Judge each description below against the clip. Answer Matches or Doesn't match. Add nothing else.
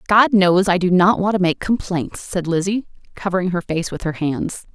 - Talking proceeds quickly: Matches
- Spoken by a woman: Matches